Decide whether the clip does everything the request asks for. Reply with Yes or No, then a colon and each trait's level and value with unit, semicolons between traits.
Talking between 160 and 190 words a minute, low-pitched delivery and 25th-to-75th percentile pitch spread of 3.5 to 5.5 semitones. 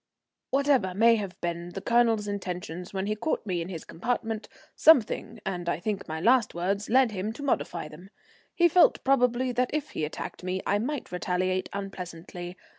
No: average, 180 wpm; high, 200 Hz; average, 5.0 semitones